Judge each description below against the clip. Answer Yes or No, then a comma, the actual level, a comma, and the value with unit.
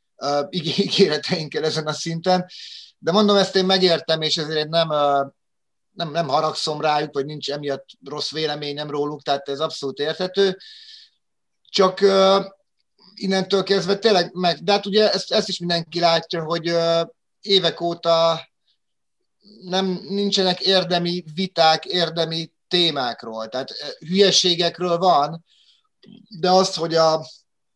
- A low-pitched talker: No, medium, 170 Hz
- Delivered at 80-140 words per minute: Yes, average, 120 wpm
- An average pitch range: Yes, average, 3.5 semitones